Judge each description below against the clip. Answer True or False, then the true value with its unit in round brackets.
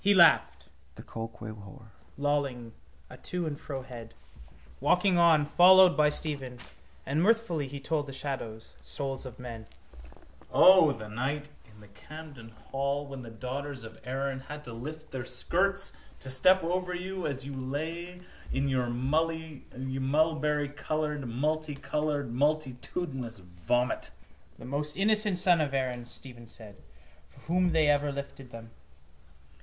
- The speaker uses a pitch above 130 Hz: True (140 Hz)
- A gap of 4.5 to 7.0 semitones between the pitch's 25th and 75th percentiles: False (3.7 semitones)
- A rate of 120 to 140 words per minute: True (135 wpm)